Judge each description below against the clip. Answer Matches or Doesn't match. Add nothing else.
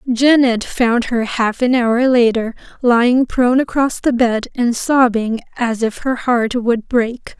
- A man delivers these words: Doesn't match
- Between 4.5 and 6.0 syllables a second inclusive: Doesn't match